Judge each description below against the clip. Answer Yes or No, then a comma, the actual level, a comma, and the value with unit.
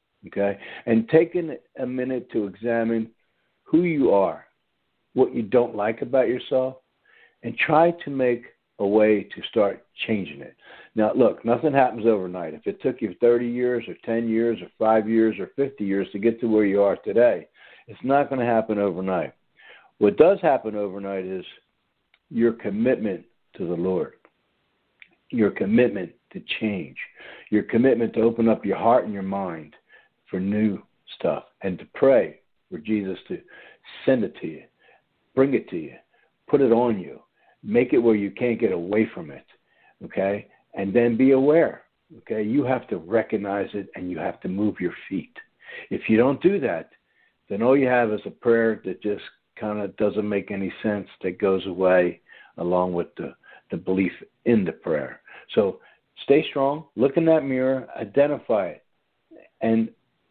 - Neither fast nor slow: Yes, average, 170 wpm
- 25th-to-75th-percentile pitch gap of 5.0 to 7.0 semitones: No, average, 3.6 semitones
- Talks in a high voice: No, low, 110 Hz